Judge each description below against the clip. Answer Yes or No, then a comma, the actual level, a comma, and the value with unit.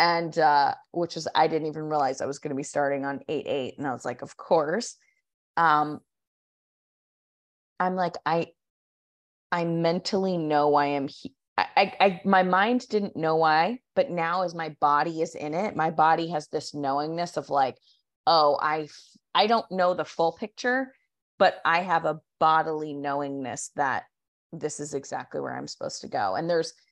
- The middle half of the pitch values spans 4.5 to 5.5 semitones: No, average, 3.2 semitones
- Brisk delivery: No, average, 180 wpm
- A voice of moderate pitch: Yes, medium, 160 Hz